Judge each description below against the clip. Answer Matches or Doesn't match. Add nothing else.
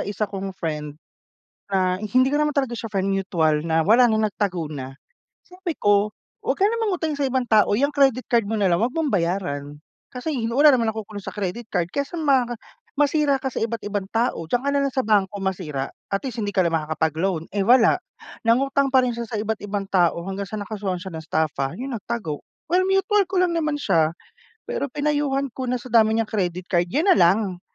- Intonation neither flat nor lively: Doesn't match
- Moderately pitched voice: Doesn't match